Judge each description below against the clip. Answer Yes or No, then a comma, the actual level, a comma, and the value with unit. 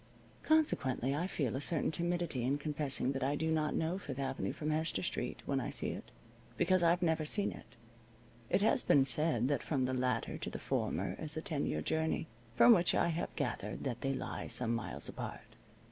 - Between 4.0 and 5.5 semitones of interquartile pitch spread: Yes, average, 4.4 semitones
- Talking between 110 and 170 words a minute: No, fast, 205 wpm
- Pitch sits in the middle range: Yes, medium, 150 Hz